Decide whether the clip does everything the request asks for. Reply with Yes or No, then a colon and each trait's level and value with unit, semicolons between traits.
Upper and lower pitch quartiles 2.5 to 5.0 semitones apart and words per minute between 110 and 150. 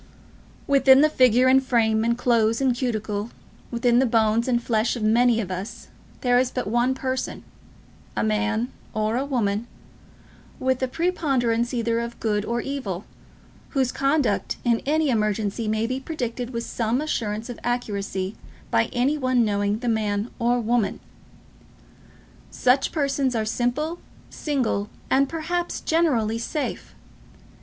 Yes: average, 3.1 semitones; average, 140 wpm